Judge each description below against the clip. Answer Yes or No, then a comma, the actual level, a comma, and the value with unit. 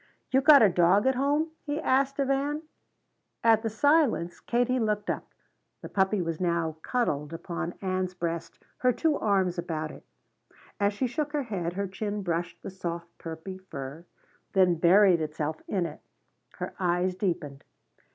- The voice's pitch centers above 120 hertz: Yes, high, 190 Hz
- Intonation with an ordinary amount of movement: No, wide, 6.4 semitones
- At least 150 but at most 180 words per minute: Yes, average, 160 wpm